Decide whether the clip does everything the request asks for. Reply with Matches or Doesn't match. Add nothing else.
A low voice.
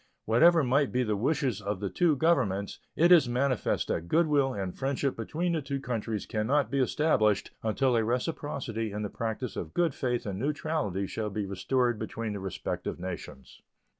Matches